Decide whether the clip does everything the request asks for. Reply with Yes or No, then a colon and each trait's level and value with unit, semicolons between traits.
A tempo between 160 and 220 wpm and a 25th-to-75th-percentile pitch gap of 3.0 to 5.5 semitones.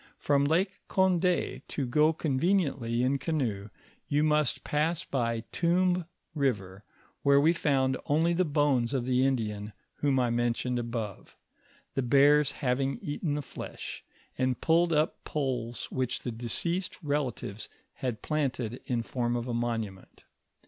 No: average, 140 wpm; average, 4.2 semitones